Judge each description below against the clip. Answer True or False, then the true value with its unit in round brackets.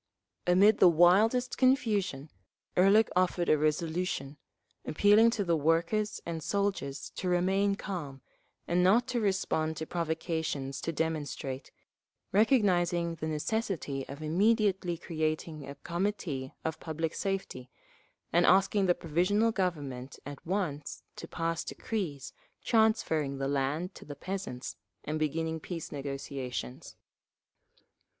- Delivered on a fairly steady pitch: False (4.7 semitones)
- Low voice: False (170 Hz)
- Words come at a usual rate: False (120 wpm)